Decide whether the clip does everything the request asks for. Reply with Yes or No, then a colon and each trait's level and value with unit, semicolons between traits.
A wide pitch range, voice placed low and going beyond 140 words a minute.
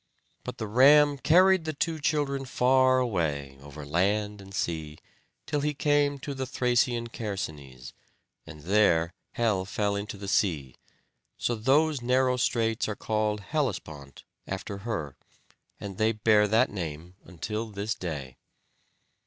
No: wide, 6.7 semitones; low, 105 Hz; slow, 135 wpm